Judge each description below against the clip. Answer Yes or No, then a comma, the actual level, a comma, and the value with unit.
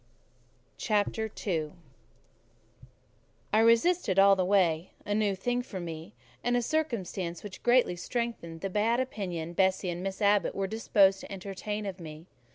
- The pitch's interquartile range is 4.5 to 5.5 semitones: No, average, 3.7 semitones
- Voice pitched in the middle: No, high, 195 Hz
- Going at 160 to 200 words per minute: No, average, 150 wpm